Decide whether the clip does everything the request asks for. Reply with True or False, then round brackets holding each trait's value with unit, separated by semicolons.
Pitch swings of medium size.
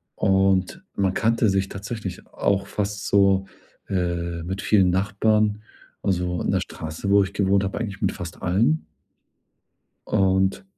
False (1.5 semitones)